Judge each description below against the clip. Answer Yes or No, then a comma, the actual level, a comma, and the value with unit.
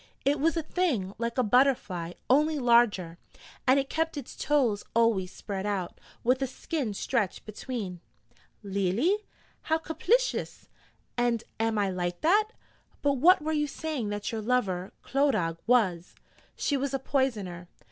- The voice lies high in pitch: Yes, high, 240 Hz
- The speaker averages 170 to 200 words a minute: No, average, 145 wpm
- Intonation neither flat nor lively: No, wide, 6.3 semitones